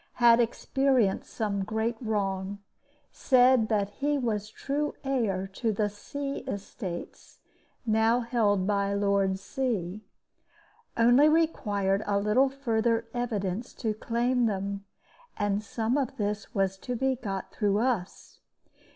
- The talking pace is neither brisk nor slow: No, slow, 125 wpm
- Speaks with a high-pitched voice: Yes, high, 220 Hz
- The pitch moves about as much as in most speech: Yes, average, 3.7 semitones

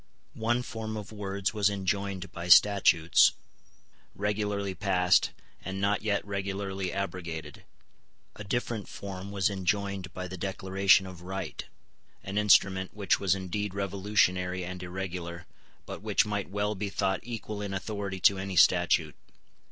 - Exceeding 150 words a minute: No, slow, 135 wpm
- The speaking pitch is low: Yes, very low, 95 Hz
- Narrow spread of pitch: Yes, narrow, 1.7 semitones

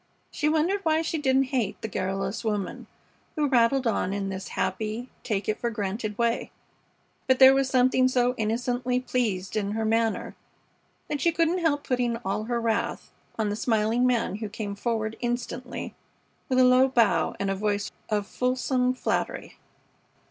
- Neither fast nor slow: Yes, average, 165 wpm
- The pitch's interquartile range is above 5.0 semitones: No, average, 3.4 semitones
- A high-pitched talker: Yes, high, 235 Hz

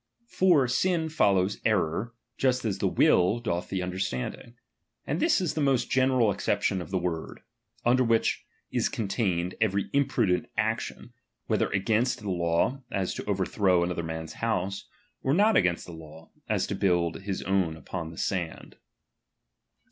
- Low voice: Yes, low, 100 Hz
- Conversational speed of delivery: Yes, average, 155 wpm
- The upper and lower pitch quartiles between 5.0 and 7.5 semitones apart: Yes, average, 5.3 semitones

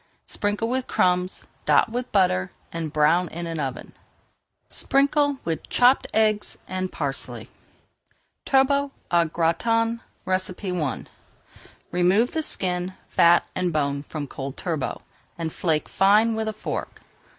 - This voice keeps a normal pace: No, slow, 125 wpm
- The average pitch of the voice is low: No, medium, 185 Hz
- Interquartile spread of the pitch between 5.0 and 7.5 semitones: Yes, wide, 5.6 semitones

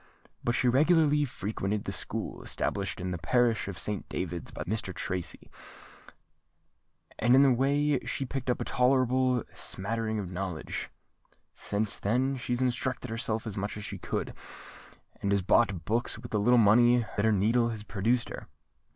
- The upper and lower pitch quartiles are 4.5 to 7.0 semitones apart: No, average, 3.8 semitones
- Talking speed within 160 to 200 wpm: Yes, average, 170 wpm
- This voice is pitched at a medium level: No, low, 115 Hz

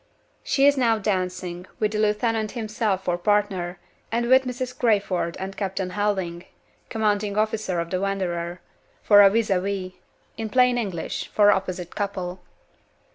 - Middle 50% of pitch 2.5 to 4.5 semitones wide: Yes, average, 3.0 semitones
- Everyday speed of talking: Yes, average, 145 wpm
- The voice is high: Yes, high, 205 Hz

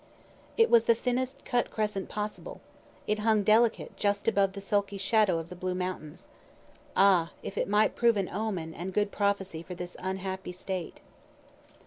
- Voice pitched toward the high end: Yes, high, 200 Hz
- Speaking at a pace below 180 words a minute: Yes, average, 165 wpm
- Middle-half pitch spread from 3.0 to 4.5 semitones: No, narrow, 2.6 semitones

